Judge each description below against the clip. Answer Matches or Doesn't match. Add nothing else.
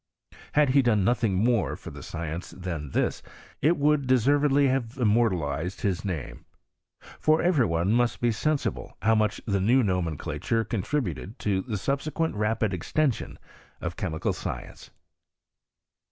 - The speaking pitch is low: Matches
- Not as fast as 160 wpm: Matches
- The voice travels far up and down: Matches